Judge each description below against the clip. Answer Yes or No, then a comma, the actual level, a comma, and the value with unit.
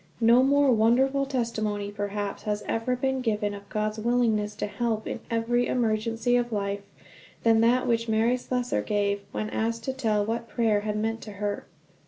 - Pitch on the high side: Yes, high, 225 Hz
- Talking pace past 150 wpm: Yes, average, 175 wpm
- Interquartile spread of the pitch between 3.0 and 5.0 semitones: No, narrow, 2.5 semitones